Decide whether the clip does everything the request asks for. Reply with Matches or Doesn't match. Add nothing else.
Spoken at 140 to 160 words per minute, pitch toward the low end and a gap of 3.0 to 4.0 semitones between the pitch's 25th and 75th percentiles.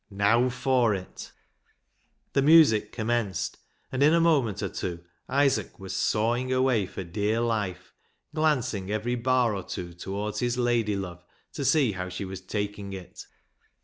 Doesn't match